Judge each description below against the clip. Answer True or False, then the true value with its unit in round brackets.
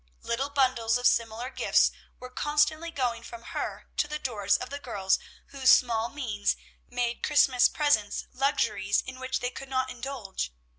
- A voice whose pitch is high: True (250 Hz)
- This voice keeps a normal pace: True (160 wpm)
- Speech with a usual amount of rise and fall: True (3.2 semitones)